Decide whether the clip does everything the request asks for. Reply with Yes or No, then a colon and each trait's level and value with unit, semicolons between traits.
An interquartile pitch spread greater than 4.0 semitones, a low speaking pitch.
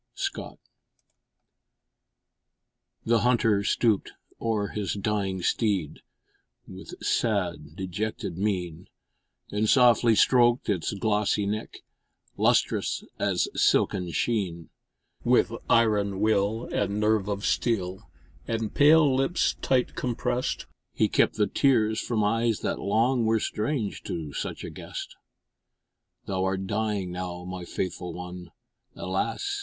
No: average, 3.4 semitones; low, 105 Hz